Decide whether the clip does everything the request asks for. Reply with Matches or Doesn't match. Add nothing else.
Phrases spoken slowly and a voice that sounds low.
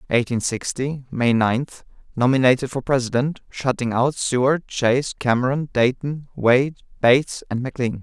Matches